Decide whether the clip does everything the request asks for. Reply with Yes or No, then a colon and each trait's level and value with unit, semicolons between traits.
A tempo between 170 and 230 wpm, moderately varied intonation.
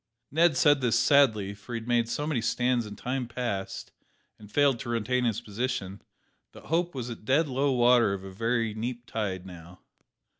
Yes: average, 190 wpm; average, 3.4 semitones